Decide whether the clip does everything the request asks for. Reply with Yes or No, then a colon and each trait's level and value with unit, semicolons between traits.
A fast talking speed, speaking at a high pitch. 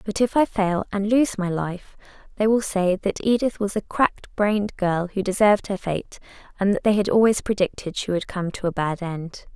Yes: fast, 220 wpm; high, 200 Hz